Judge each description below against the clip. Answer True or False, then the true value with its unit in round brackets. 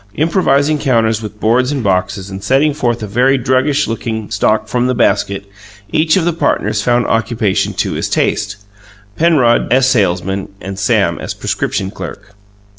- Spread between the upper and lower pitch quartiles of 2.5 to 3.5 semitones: False (4.9 semitones)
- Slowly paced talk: False (160 wpm)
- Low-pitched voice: True (115 Hz)